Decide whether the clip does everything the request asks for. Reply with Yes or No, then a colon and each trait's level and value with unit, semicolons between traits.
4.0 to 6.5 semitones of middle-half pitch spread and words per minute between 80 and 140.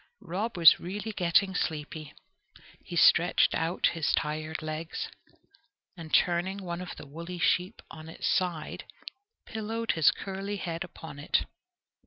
No: average, 3.1 semitones; slow, 135 wpm